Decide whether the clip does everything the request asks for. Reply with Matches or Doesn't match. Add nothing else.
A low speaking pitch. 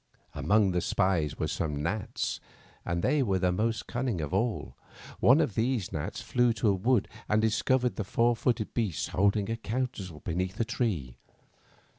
Matches